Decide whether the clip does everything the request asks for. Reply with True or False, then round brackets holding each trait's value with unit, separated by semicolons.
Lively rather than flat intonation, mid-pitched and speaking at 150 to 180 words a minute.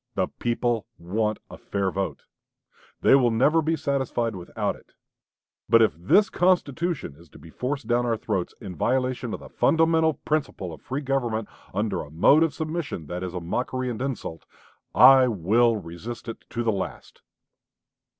False (5.9 semitones; 120 Hz; 170 wpm)